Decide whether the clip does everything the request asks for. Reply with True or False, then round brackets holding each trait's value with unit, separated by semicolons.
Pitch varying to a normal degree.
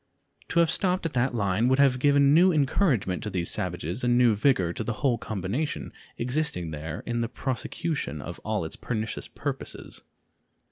False (6.6 semitones)